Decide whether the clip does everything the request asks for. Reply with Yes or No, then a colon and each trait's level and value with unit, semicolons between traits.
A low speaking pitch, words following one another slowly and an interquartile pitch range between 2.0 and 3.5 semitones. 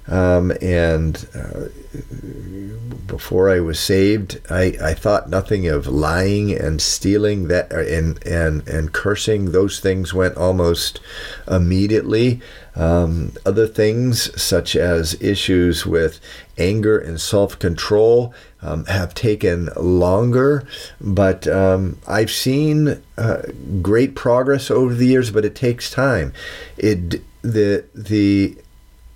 No: very low, 95 Hz; slow, 115 wpm; average, 4.1 semitones